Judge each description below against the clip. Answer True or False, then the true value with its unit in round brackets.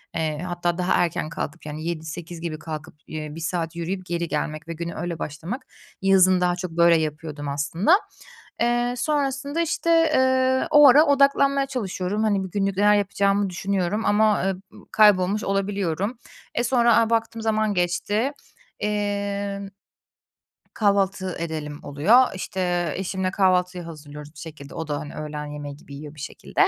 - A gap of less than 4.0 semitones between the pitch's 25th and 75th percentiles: False (4.7 semitones)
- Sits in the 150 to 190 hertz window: True (185 Hz)